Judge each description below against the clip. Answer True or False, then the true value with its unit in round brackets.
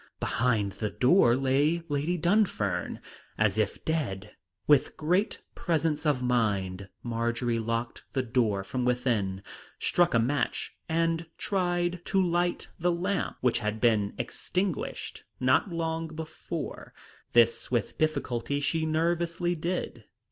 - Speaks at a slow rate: True (125 wpm)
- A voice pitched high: False (140 Hz)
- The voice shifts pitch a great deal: True (6.5 semitones)